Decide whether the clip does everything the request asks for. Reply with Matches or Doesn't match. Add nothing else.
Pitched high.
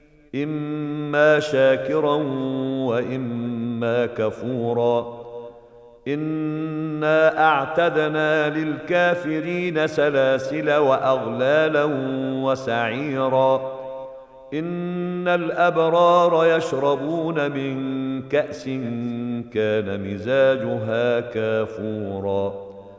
Doesn't match